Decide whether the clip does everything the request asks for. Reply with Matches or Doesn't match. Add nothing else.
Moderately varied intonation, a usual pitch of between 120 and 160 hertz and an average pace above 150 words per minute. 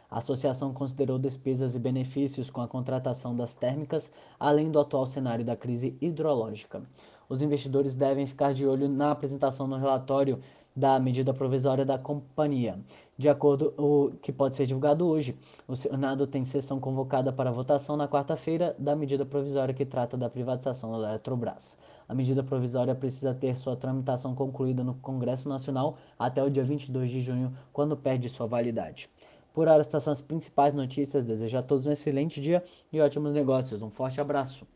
Doesn't match